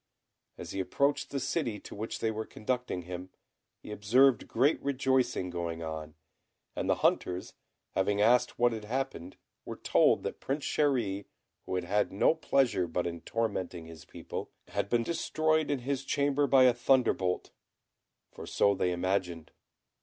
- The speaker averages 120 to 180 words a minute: Yes, average, 160 wpm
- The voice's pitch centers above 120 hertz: No, low, 110 Hz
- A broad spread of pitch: Yes, wide, 6.7 semitones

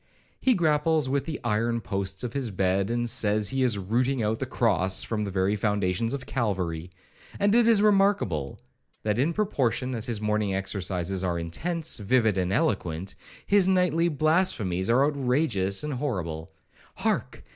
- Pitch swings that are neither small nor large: No, wide, 6.9 semitones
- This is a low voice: Yes, low, 115 Hz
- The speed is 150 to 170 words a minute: Yes, average, 155 wpm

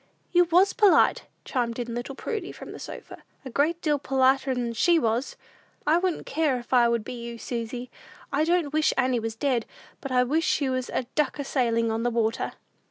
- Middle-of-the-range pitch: No, very high, 260 Hz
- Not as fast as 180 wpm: No, average, 200 wpm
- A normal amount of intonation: Yes, average, 4.4 semitones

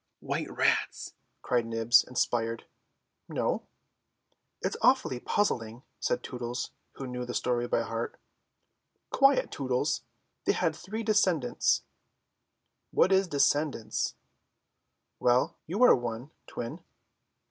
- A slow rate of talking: Yes, slow, 105 wpm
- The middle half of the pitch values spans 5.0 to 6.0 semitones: Yes, wide, 5.4 semitones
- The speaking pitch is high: No, low, 125 Hz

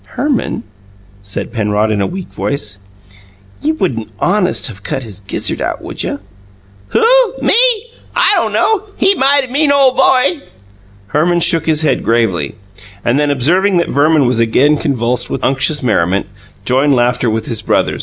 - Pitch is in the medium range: Yes, medium, 145 Hz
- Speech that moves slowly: No, average, 160 wpm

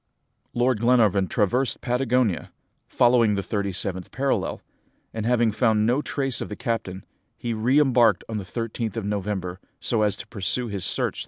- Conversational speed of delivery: Yes, average, 180 wpm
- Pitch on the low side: Yes, low, 115 Hz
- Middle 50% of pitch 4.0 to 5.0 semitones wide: No, average, 3.4 semitones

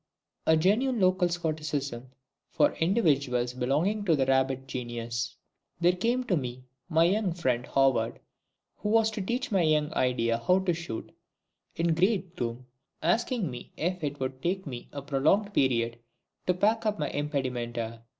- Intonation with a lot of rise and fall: Yes, wide, 6.6 semitones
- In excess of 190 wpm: No, average, 155 wpm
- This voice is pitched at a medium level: Yes, medium, 155 Hz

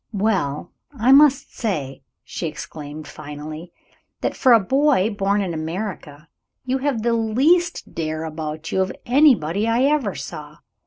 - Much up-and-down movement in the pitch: Yes, wide, 8.4 semitones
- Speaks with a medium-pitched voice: No, high, 195 Hz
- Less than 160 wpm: Yes, average, 145 wpm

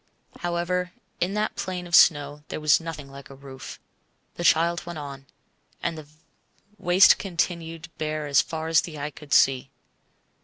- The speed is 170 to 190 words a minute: No, average, 155 wpm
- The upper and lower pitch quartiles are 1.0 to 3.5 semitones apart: Yes, average, 3.0 semitones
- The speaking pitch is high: No, medium, 160 Hz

